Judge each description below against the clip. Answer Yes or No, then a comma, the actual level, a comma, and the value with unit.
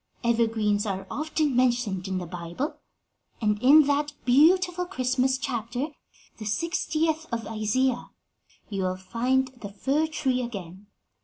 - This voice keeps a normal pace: No, slow, 130 wpm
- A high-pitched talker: Yes, high, 245 Hz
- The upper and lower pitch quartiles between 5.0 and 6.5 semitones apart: Yes, wide, 5.6 semitones